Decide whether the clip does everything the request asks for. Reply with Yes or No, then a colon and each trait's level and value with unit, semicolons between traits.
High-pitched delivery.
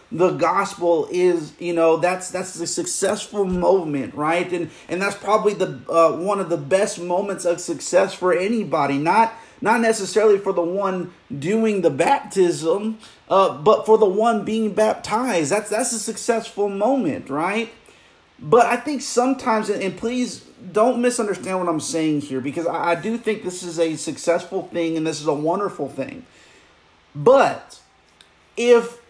Yes: high, 195 Hz